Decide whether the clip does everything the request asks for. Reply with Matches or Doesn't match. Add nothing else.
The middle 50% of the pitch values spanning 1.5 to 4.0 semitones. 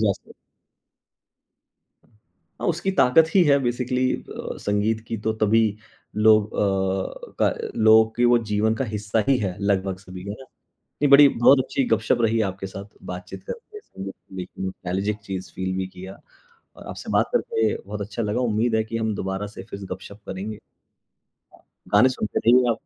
Matches